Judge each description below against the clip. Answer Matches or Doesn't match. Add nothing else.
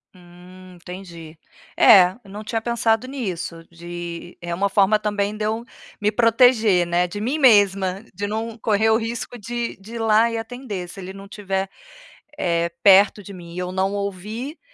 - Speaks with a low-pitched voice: Doesn't match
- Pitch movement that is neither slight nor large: Matches